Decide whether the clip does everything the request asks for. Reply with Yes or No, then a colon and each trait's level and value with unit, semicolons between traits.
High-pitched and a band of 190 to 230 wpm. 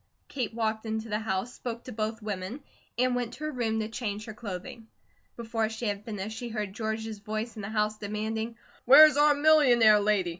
Yes: high, 220 Hz; average, 195 wpm